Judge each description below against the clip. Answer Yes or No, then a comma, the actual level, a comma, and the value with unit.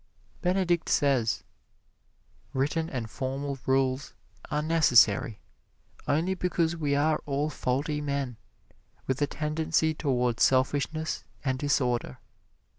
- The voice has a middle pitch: Yes, medium, 145 Hz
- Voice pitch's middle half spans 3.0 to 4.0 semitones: Yes, average, 3.4 semitones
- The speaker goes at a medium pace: No, slow, 105 wpm